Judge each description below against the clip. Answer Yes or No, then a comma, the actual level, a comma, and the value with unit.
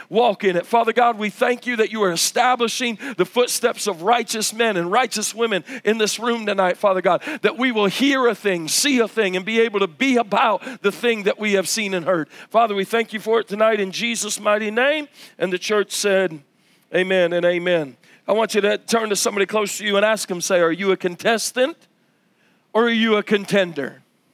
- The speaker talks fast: Yes, fast, 220 wpm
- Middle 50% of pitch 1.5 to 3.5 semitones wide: Yes, average, 3.2 semitones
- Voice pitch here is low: No, high, 215 Hz